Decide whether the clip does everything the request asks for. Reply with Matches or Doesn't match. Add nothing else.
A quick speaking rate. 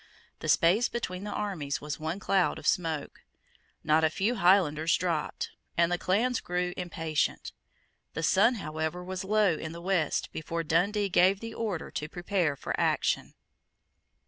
Doesn't match